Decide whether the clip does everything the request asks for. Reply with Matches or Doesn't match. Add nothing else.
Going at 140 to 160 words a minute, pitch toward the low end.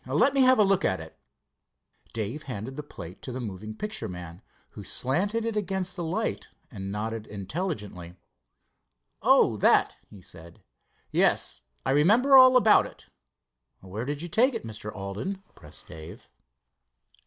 Matches